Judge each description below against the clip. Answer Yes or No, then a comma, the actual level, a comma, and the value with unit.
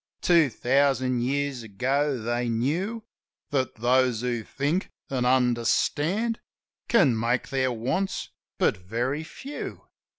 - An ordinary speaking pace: No, slow, 110 wpm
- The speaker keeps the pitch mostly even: No, average, 3.4 semitones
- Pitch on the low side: Yes, low, 130 Hz